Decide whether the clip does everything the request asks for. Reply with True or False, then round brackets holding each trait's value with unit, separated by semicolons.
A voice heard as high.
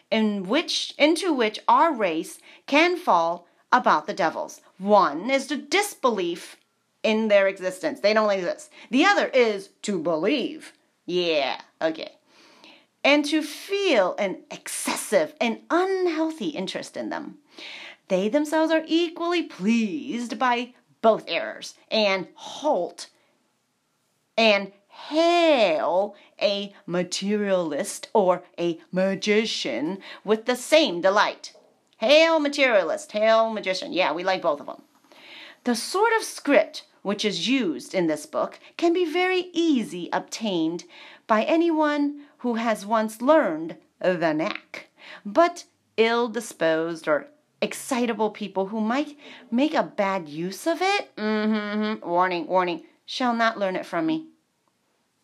True (270 Hz)